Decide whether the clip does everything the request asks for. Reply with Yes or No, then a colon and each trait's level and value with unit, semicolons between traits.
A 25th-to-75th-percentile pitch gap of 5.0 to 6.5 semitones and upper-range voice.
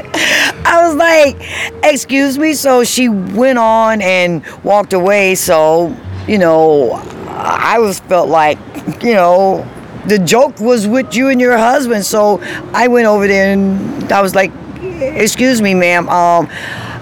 Yes: average, 5.3 semitones; high, 210 Hz